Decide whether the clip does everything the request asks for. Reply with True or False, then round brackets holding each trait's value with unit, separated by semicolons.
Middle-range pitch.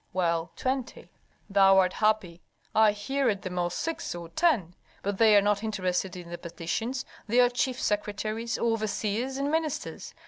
False (210 Hz)